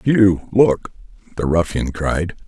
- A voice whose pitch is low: Yes, very low, 95 Hz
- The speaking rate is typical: No, slow, 120 wpm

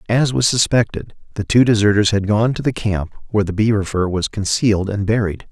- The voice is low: Yes, low, 105 Hz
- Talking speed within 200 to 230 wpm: Yes, fast, 205 wpm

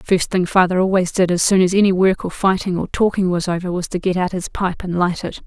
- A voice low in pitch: No, medium, 185 Hz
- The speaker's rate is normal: No, fast, 275 wpm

